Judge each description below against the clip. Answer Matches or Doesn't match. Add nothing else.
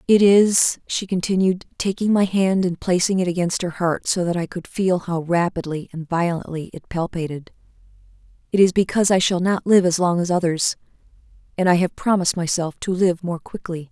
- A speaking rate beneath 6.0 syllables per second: Matches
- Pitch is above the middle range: Doesn't match